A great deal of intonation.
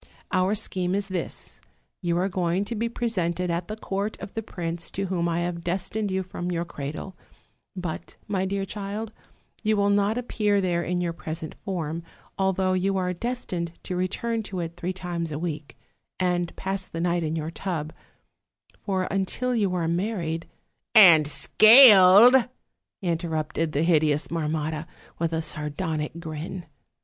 No: average, 3.0 semitones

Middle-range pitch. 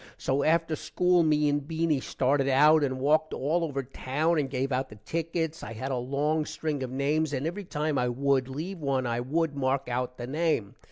Yes: medium, 145 Hz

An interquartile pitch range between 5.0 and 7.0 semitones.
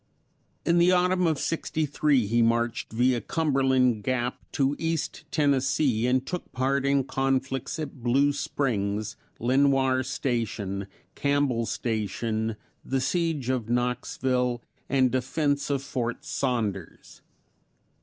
No: average, 3.1 semitones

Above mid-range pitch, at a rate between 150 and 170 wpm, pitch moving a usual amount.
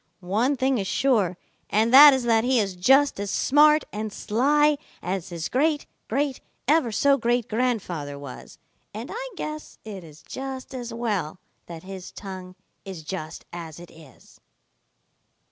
No: high, 225 Hz; average, 155 wpm; wide, 6.6 semitones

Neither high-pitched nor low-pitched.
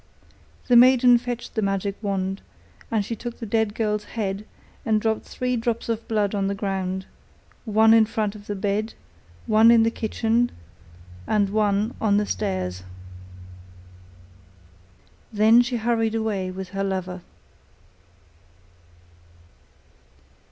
No: high, 215 Hz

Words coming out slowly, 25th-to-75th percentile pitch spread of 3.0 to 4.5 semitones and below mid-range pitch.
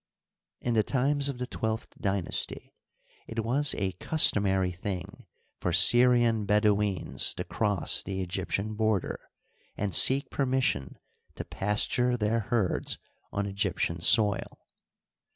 Yes: slow, 115 wpm; average, 3.8 semitones; low, 105 Hz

